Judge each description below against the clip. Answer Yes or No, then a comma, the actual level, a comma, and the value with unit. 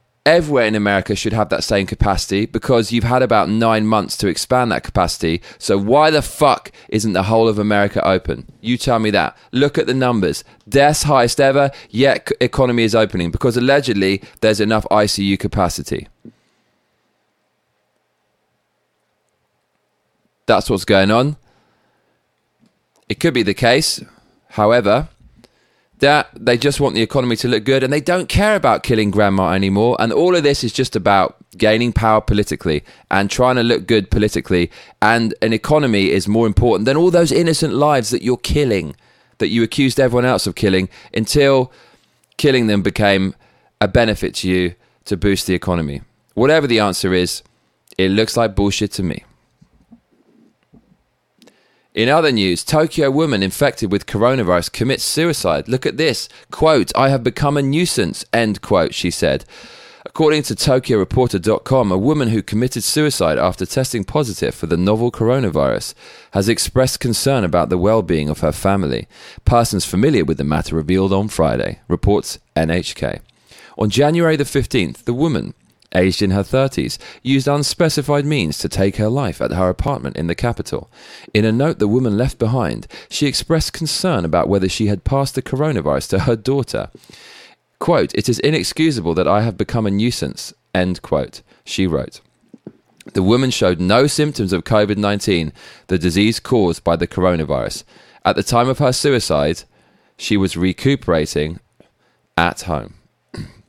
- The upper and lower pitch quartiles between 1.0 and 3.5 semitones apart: No, average, 5.1 semitones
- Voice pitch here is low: Yes, low, 110 Hz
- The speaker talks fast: No, average, 160 wpm